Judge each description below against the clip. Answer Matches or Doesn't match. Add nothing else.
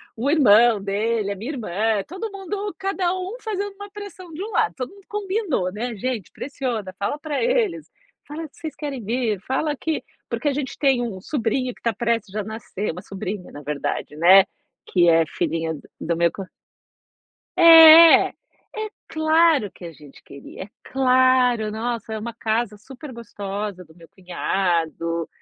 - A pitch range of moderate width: Doesn't match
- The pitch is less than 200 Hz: Doesn't match